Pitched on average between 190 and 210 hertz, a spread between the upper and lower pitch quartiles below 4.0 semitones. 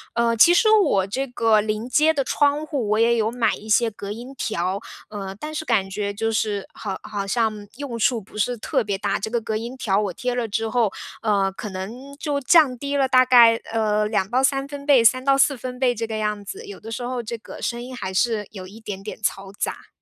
No: high, 225 Hz; average, 3.6 semitones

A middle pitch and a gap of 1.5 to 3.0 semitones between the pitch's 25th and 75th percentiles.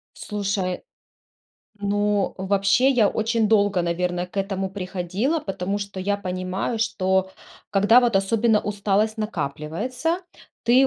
No: high, 200 Hz; average, 2.7 semitones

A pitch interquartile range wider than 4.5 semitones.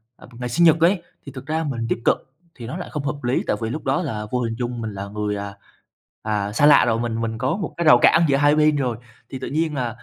Yes: average, 4.9 semitones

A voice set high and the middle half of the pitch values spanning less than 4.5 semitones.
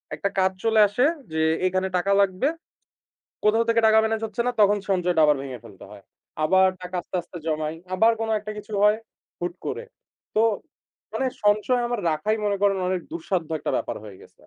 Yes: high, 195 Hz; average, 4.0 semitones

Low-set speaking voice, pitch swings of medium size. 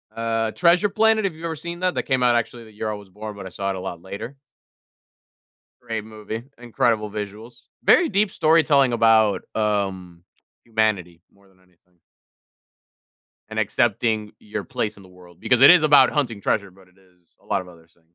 Yes: low, 110 Hz; average, 4.6 semitones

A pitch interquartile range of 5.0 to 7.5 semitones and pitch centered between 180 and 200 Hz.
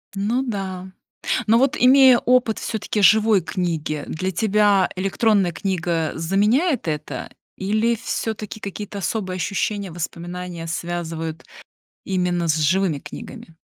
No: average, 4.0 semitones; high, 190 Hz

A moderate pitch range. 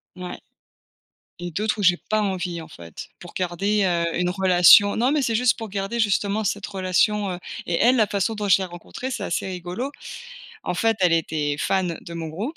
Yes: average, 3.3 semitones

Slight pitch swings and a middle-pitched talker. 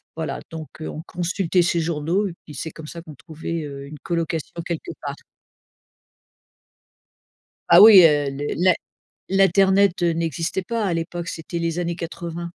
Yes: narrow, 2.0 semitones; medium, 170 Hz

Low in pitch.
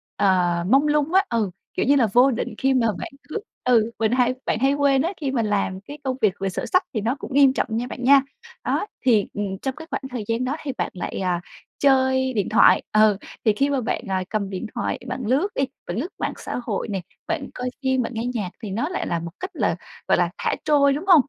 No: very high, 250 Hz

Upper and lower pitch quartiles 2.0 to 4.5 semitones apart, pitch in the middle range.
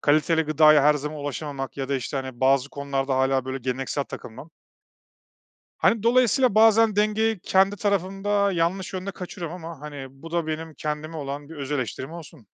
No: wide, 5.5 semitones; medium, 155 Hz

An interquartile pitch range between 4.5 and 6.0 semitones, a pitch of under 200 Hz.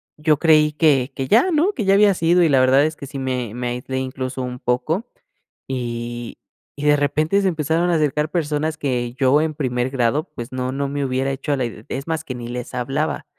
No: average, 3.7 semitones; medium, 140 Hz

